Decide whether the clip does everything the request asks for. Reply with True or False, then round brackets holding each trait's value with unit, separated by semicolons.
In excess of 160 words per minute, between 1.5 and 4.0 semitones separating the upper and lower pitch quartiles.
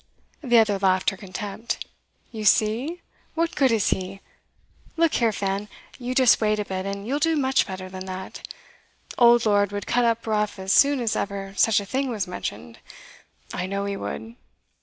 True (180 wpm; 3.7 semitones)